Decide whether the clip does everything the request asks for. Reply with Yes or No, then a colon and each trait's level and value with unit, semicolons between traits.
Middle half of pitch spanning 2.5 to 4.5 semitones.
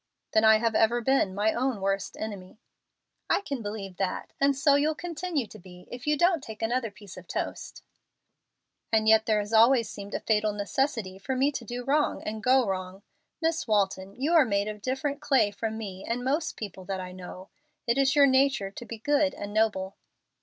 No: average, 5.1 semitones